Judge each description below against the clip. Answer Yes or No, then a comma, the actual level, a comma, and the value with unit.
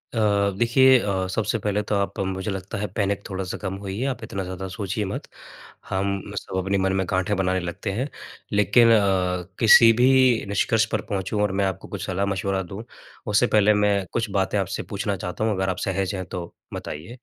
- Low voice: Yes, low, 100 Hz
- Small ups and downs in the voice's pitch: Yes, narrow, 2.0 semitones